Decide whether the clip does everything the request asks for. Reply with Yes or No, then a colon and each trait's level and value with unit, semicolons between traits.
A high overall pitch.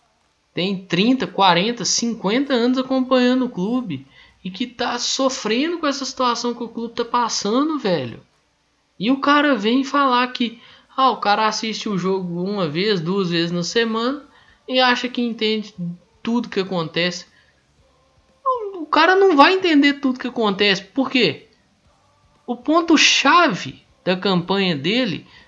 Yes: high, 235 Hz